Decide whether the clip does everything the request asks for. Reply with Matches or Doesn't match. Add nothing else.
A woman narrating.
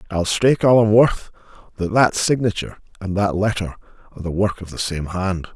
Doesn't match